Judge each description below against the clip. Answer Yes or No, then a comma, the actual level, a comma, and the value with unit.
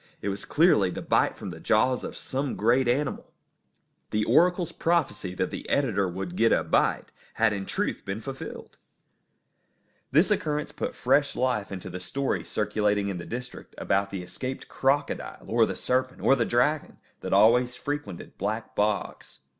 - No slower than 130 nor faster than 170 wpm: Yes, average, 165 wpm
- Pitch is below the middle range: Yes, low, 115 Hz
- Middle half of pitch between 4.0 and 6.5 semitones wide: Yes, average, 5.3 semitones